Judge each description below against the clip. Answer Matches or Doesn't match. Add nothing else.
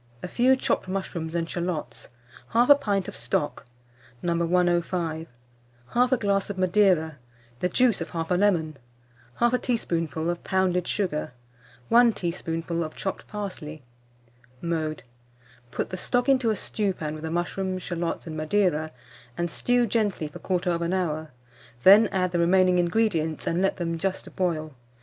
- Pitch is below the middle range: Doesn't match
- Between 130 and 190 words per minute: Matches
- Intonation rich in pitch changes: Doesn't match